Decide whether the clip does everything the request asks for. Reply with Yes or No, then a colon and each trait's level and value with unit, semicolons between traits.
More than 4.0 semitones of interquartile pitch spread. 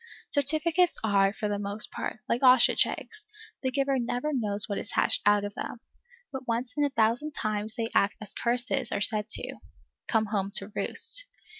Yes: average, 4.7 semitones